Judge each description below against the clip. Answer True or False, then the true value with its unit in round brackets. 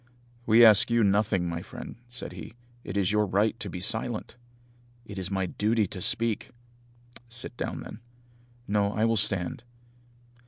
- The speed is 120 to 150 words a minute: False (160 wpm)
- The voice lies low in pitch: True (105 Hz)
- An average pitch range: True (3.0 semitones)